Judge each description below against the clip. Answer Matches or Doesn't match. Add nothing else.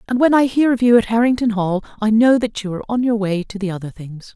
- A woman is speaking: Matches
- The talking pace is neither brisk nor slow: Doesn't match